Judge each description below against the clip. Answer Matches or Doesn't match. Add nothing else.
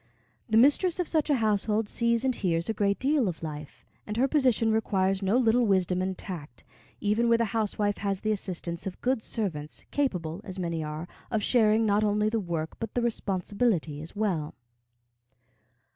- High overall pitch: Matches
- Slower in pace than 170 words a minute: Doesn't match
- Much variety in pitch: Doesn't match